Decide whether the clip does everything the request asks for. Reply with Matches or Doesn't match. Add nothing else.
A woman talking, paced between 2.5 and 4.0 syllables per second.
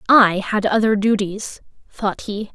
Matches